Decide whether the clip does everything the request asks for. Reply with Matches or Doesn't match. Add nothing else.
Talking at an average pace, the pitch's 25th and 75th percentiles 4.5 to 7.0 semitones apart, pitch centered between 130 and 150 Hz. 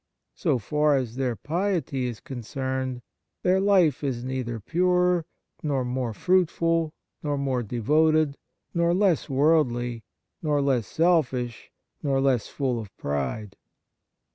Doesn't match